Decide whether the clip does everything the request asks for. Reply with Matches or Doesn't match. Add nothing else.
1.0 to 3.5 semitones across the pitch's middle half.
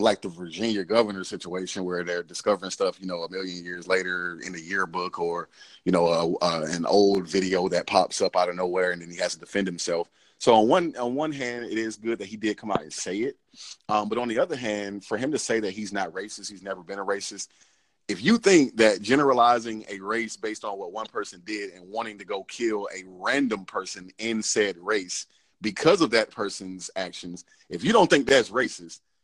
Matches